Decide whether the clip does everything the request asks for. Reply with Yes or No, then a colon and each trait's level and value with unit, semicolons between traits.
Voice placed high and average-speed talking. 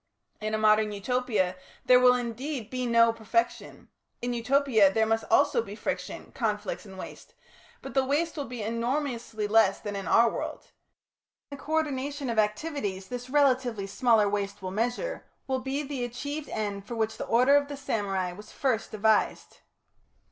Yes: high, 230 Hz; average, 170 wpm